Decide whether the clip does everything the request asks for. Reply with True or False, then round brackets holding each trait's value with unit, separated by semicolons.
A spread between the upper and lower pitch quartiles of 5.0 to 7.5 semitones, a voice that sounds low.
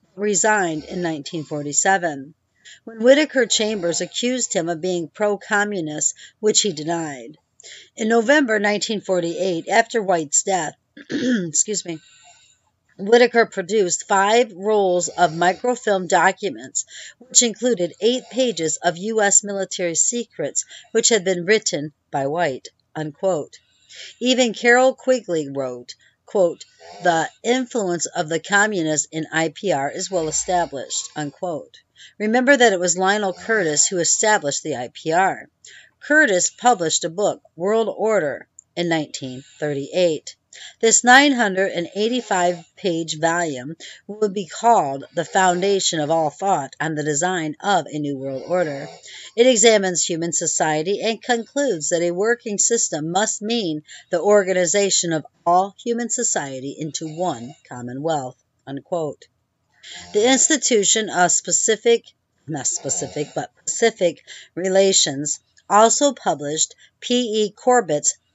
False (5.5 semitones; 185 Hz)